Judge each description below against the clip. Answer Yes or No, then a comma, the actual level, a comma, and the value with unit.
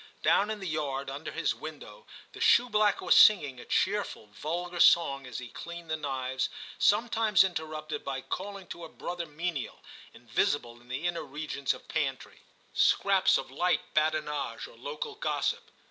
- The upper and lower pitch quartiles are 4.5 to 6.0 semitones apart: Yes, wide, 5.4 semitones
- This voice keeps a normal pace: Yes, average, 160 wpm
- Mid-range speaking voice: Yes, medium, 155 Hz